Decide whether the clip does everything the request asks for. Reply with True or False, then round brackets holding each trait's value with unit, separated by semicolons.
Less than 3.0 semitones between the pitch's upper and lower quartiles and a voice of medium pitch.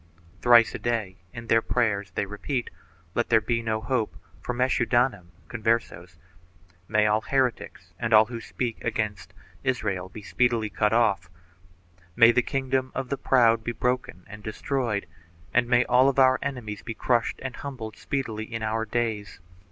False (2.6 semitones; 115 Hz)